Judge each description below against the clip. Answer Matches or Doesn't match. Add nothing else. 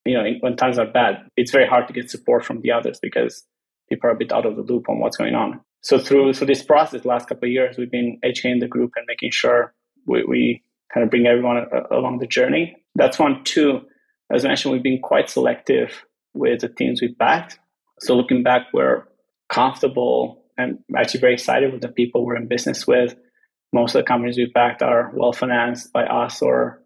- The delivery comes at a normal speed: Doesn't match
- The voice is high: Doesn't match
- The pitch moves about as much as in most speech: Doesn't match